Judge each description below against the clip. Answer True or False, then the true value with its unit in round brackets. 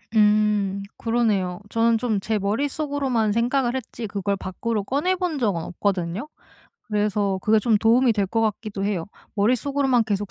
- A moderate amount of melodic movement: True (3.2 semitones)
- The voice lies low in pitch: False (215 Hz)